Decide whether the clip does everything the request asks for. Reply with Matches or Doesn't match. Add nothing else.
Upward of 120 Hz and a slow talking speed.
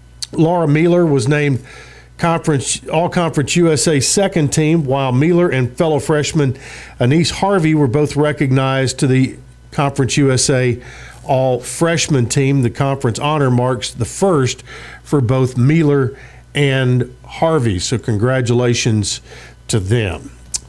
Matches